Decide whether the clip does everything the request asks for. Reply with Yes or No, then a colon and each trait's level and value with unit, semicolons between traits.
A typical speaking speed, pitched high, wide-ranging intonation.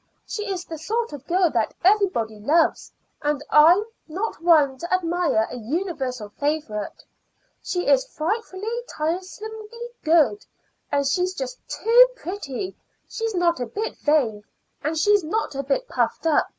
Yes: average, 150 wpm; very high, 340 Hz; wide, 6.1 semitones